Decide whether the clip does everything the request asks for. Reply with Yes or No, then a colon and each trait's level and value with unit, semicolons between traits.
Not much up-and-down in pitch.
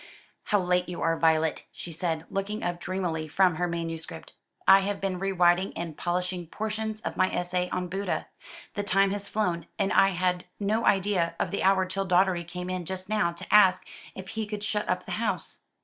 Yes: narrow, 2.1 semitones